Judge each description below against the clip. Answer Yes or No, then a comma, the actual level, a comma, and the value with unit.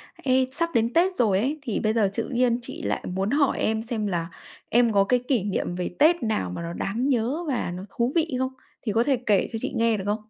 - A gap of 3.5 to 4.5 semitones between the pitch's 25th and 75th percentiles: Yes, average, 4.1 semitones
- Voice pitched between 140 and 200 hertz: No, high, 230 Hz